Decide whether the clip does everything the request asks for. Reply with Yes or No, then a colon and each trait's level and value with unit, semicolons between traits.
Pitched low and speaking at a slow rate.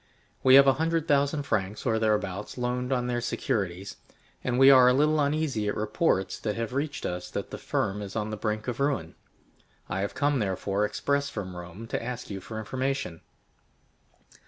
No: low, 115 Hz; average, 185 wpm